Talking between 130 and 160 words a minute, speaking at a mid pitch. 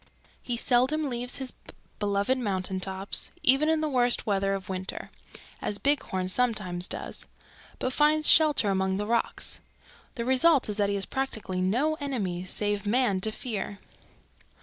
No: average, 150 wpm; high, 220 Hz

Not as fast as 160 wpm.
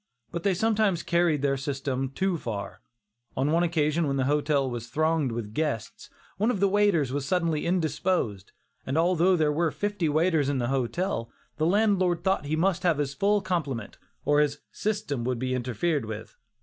No: average, 180 wpm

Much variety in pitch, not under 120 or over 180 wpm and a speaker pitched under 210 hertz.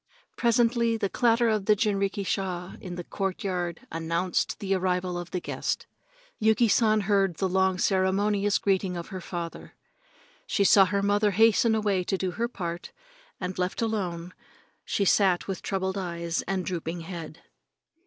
No: narrow, 2.6 semitones; average, 155 wpm; high, 190 Hz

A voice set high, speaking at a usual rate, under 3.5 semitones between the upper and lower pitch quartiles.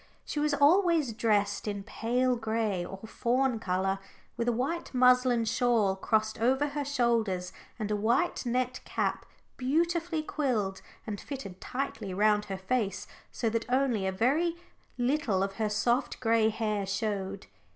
No: high, 230 Hz; average, 150 wpm; average, 4.1 semitones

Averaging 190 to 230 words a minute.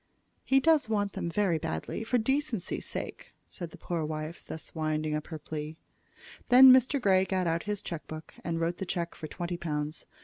Yes: average, 195 wpm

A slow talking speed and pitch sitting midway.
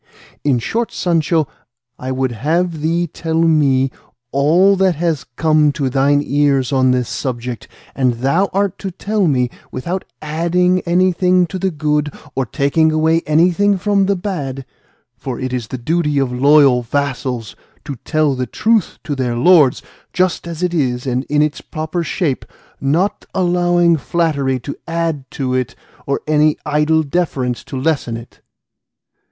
No: average, 155 wpm; medium, 150 Hz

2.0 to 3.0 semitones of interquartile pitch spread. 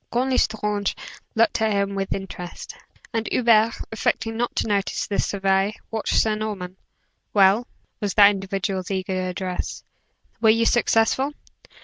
Yes: narrow, 2.6 semitones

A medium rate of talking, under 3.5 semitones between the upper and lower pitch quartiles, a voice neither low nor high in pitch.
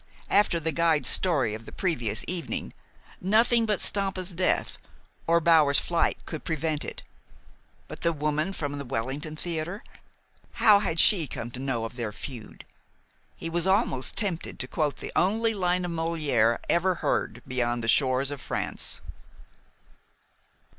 No: average, 150 wpm; wide, 5.4 semitones; medium, 160 Hz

